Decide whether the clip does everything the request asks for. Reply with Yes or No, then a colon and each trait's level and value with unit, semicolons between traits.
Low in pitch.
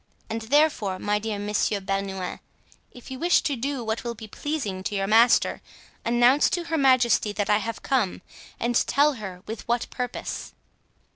No: high, 230 Hz